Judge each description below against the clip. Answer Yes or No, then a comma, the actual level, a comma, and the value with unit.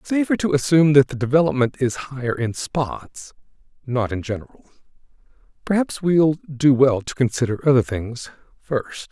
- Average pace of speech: Yes, average, 145 wpm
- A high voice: No, low, 135 Hz